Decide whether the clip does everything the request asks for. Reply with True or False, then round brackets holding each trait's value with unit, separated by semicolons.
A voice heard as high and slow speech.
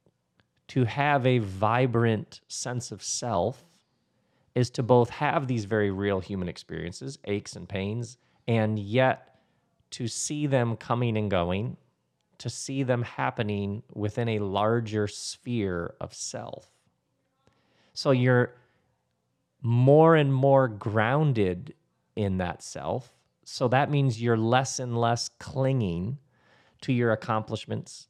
False (115 Hz; 120 wpm)